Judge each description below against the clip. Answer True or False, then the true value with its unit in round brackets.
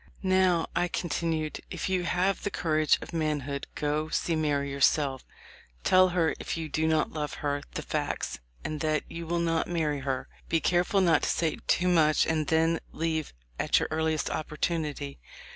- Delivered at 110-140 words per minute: False (175 wpm)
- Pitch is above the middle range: False (160 Hz)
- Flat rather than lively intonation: True (2.1 semitones)